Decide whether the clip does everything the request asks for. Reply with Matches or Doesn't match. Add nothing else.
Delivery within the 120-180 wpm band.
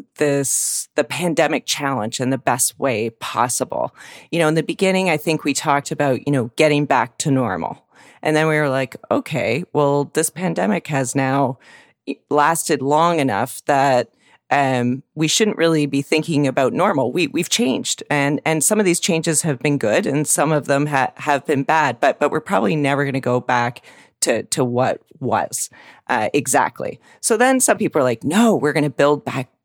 Doesn't match